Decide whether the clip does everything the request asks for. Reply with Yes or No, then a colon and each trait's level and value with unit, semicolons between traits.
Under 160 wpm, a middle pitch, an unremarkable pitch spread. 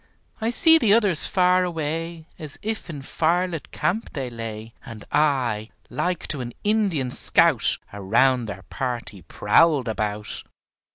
No: slow, 135 wpm; medium, 145 Hz; wide, 7.6 semitones